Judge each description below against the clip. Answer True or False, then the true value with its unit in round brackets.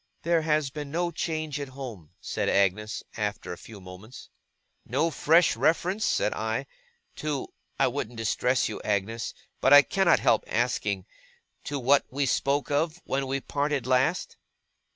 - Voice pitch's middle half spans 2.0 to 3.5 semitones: False (5.3 semitones)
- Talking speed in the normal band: True (150 wpm)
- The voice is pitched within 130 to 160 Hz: True (135 Hz)